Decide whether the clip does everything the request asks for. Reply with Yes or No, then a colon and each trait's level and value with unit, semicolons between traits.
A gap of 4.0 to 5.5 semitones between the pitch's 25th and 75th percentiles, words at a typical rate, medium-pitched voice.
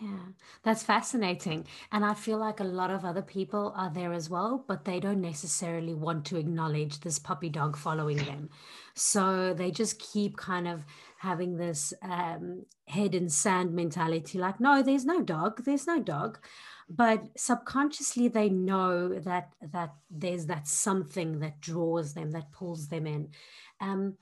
No: average, 3.5 semitones; average, 165 wpm; medium, 180 Hz